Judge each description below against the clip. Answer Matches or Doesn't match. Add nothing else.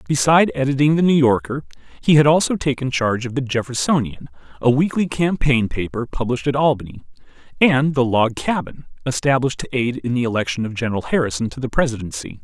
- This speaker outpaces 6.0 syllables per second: Matches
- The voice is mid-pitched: Doesn't match